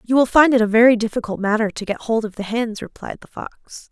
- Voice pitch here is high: Yes, high, 225 Hz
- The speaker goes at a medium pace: No, fast, 260 wpm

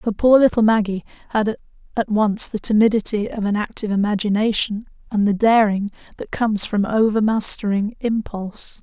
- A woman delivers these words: Yes, female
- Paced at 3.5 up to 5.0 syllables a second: No, 5.4 syllables/s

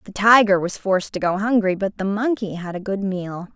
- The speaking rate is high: Yes, fast, 235 wpm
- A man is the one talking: No, female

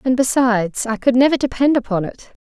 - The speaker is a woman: Yes, female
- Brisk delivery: No, average, 195 wpm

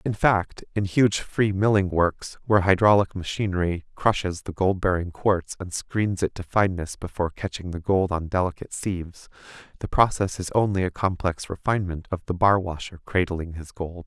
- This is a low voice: Yes, very low, 95 Hz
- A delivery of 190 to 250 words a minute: No, average, 175 wpm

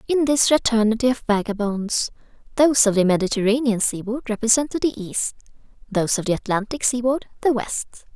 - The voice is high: Yes, high, 230 Hz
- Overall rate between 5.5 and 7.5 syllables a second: Yes, 5.8 syllables/s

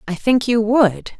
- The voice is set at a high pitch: Yes, high, 220 Hz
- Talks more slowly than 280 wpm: Yes, average, 200 wpm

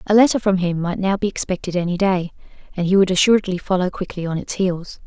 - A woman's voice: Yes, female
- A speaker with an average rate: No, fast, 225 wpm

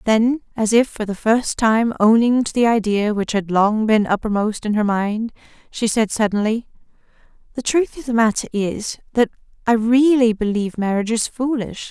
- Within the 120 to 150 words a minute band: No, average, 175 wpm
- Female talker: Yes, female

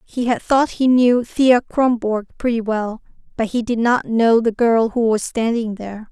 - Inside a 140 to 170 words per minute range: No, average, 195 wpm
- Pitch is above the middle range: Yes, high, 230 Hz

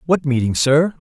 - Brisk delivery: No, average, 165 wpm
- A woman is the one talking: No, male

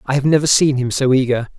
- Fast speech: Yes, fast, 265 wpm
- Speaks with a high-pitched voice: No, low, 135 Hz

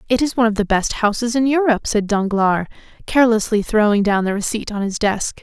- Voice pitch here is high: Yes, high, 220 Hz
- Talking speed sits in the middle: No, fast, 210 wpm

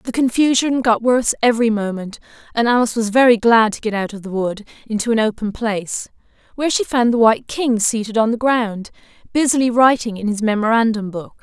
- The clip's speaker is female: Yes, female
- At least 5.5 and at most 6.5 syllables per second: Yes, 5.9 syllables/s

